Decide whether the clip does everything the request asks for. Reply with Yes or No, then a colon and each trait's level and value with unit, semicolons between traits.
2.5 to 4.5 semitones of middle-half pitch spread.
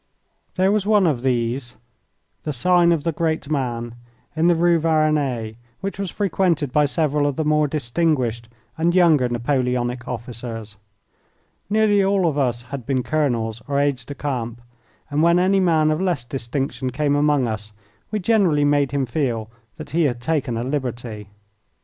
No: average, 5.2 semitones